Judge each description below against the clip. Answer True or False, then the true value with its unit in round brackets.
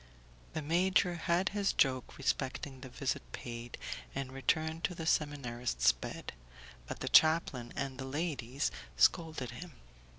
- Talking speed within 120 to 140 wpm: True (135 wpm)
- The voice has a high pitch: False (140 Hz)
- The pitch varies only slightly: False (4.3 semitones)